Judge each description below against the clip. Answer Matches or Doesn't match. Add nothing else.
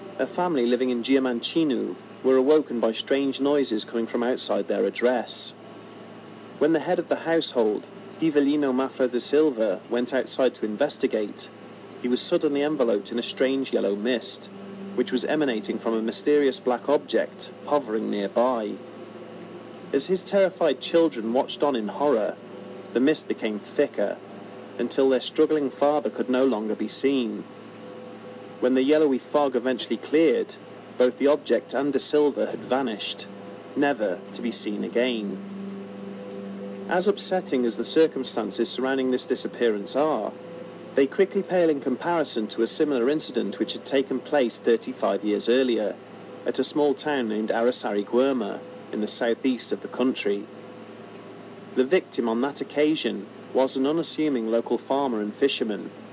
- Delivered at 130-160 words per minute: Matches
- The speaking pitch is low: Matches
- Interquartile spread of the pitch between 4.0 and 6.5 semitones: Matches